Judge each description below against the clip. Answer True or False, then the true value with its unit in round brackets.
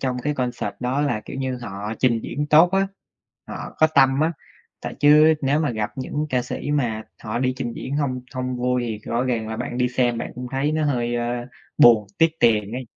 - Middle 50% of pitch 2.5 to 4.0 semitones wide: True (3.3 semitones)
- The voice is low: True (125 Hz)